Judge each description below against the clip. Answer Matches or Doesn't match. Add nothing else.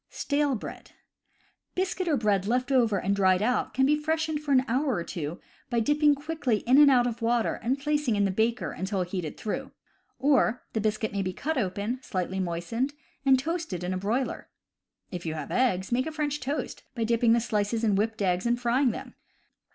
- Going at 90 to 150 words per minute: Doesn't match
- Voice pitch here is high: Matches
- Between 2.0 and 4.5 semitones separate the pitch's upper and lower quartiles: Doesn't match